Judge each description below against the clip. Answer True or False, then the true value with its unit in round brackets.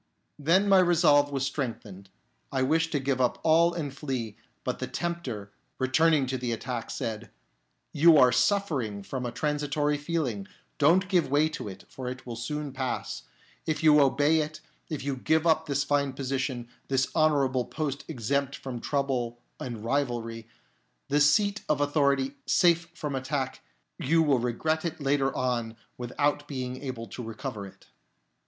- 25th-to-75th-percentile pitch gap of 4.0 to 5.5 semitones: False (3.4 semitones)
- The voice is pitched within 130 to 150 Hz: True (140 Hz)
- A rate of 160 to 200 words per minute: True (165 wpm)